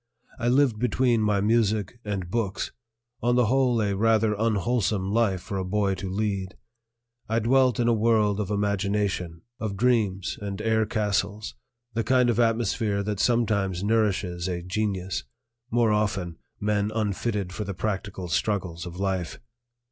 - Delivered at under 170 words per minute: Yes, average, 150 wpm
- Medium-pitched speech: No, low, 105 Hz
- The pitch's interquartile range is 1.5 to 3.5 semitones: Yes, average, 2.7 semitones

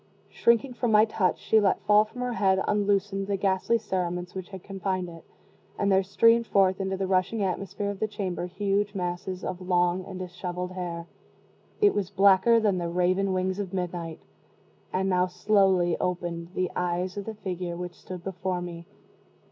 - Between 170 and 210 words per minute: Yes, average, 180 wpm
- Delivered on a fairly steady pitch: Yes, narrow, 2.1 semitones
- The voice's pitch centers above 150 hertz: Yes, high, 190 Hz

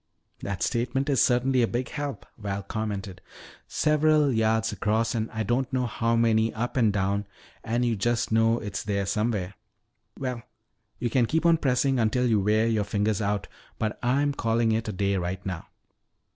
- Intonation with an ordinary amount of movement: Yes, average, 3.2 semitones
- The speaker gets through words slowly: No, average, 175 wpm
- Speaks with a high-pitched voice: No, low, 115 Hz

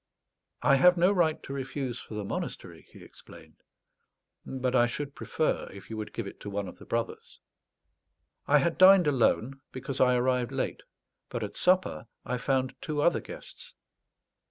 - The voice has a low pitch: Yes, low, 130 Hz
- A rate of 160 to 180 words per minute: Yes, average, 170 wpm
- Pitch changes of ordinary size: Yes, average, 4.3 semitones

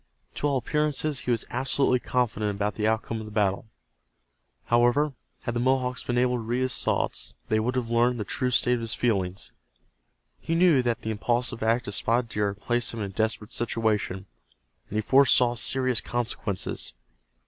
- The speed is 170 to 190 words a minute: Yes, average, 185 wpm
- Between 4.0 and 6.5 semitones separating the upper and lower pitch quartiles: No, average, 2.7 semitones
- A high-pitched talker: No, low, 120 Hz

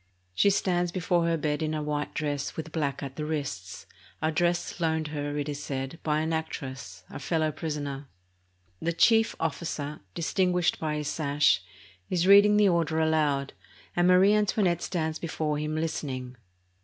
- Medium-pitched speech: Yes, medium, 155 Hz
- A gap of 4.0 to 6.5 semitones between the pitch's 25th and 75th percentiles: No, average, 2.8 semitones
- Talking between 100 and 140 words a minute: No, average, 165 wpm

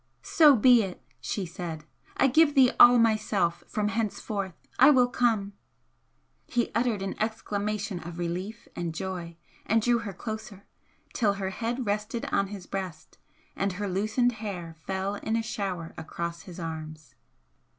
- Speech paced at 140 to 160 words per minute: Yes, average, 150 wpm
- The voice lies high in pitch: Yes, high, 205 Hz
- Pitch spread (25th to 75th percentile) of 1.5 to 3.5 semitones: No, average, 3.9 semitones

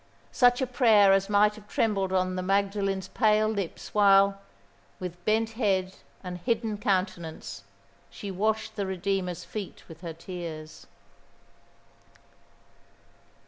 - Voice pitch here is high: Yes, high, 195 Hz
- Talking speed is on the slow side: Yes, slow, 120 wpm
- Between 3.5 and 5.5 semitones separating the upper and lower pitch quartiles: No, narrow, 2.5 semitones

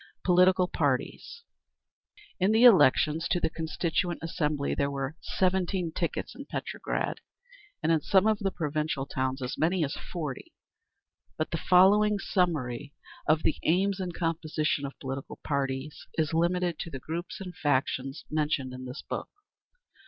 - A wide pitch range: No, average, 4.4 semitones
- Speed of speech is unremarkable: Yes, average, 145 wpm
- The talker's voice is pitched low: No, medium, 160 Hz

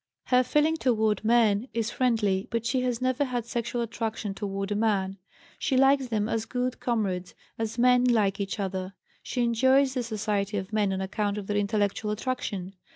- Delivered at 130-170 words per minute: No, average, 180 wpm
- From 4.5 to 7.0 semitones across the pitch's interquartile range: No, average, 3.6 semitones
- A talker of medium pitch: No, high, 220 Hz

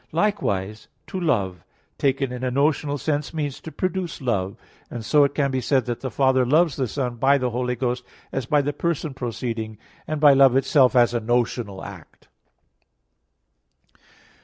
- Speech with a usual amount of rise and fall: Yes, average, 3.3 semitones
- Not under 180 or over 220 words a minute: No, average, 170 wpm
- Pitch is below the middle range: Yes, low, 130 Hz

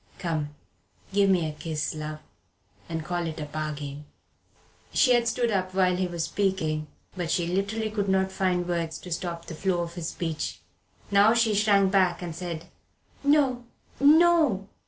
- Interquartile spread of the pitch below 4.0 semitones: Yes, average, 3.6 semitones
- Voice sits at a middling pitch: Yes, medium, 180 Hz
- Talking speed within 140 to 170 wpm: Yes, average, 165 wpm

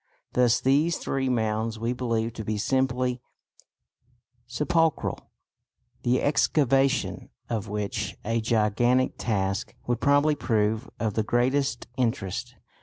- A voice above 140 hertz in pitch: No, low, 120 Hz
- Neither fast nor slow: No, slow, 110 wpm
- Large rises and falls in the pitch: No, average, 3.2 semitones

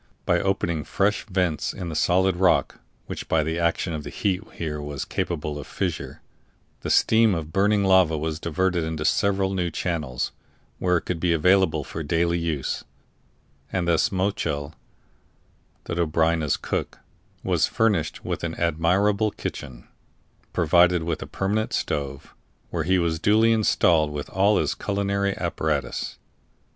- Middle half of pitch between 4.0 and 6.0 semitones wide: No, average, 3.5 semitones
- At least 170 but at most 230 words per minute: No, average, 150 wpm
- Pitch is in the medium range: No, very low, 85 Hz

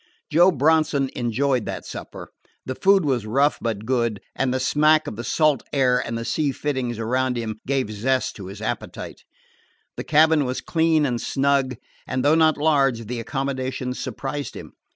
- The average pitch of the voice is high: No, low, 130 Hz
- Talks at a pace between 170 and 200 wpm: Yes, average, 175 wpm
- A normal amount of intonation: Yes, average, 3.6 semitones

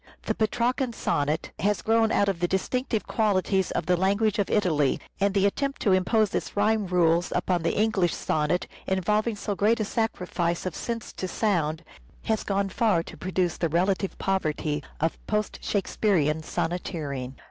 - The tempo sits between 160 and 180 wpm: Yes, average, 165 wpm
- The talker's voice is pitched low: No, high, 190 Hz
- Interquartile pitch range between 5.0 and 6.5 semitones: No, average, 3.9 semitones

